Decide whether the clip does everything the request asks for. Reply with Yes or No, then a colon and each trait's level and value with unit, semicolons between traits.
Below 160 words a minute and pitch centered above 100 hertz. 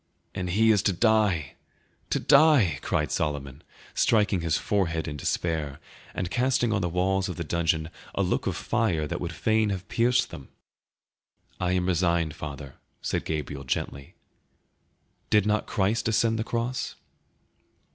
No: average, 150 wpm; very low, 90 Hz